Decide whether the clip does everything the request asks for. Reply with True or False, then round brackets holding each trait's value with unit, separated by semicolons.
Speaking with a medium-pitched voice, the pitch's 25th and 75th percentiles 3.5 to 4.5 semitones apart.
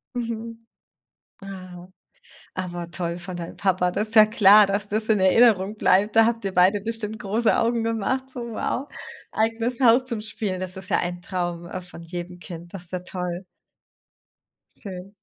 False (195 Hz; 3.9 semitones)